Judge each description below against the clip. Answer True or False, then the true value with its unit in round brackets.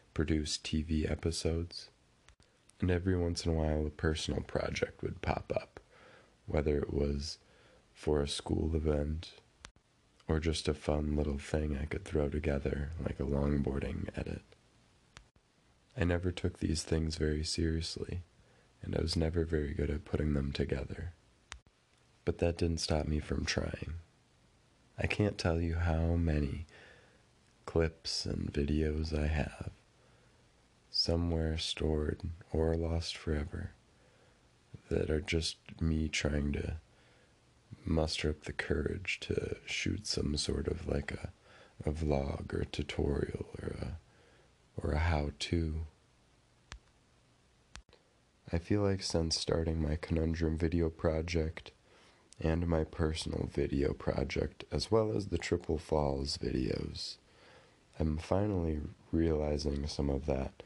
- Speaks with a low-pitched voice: True (80 Hz)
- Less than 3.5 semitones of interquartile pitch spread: True (2.7 semitones)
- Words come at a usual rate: False (130 wpm)